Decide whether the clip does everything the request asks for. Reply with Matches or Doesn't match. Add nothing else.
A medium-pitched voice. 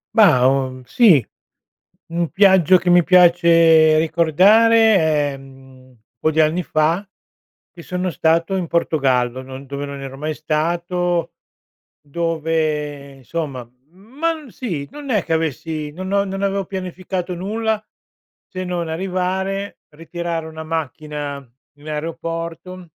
Matches